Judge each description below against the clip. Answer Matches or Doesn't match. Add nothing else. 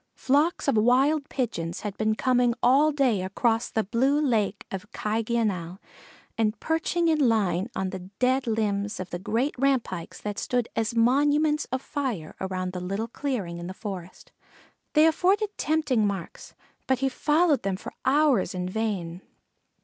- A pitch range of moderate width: Doesn't match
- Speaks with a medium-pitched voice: Doesn't match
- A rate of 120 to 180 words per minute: Matches